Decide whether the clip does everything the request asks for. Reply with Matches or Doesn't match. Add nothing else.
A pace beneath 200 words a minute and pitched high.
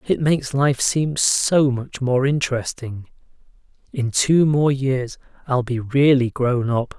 Doesn't match